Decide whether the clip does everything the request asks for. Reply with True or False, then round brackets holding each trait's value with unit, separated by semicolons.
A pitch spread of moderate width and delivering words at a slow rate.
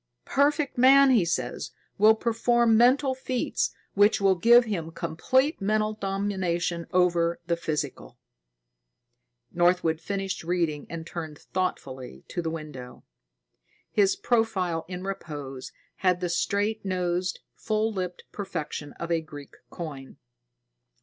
True (4.7 semitones; 120 wpm)